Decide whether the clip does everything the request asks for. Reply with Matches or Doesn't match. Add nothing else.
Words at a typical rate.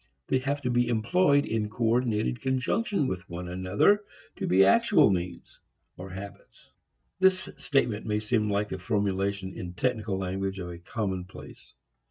Matches